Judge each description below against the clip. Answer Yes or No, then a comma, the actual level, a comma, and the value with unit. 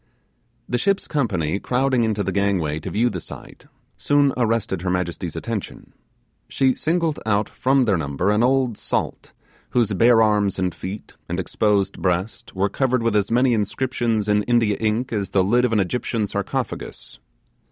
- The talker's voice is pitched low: Yes, low, 110 Hz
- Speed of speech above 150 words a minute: Yes, average, 165 wpm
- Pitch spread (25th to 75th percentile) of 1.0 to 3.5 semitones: No, average, 4.1 semitones